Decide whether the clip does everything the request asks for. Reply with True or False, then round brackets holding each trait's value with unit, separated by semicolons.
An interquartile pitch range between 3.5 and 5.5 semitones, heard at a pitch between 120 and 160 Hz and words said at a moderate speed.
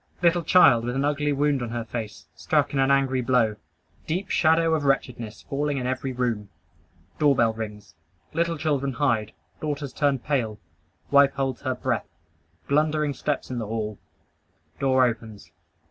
True (3.8 semitones; 135 Hz; 155 wpm)